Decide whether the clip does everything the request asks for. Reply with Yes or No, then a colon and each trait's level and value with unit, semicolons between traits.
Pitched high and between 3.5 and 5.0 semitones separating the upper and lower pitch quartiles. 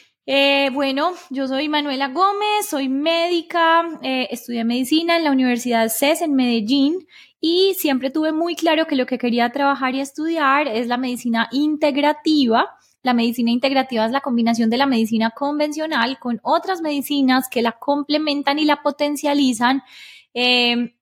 Yes: very high, 280 Hz; average, 3.9 semitones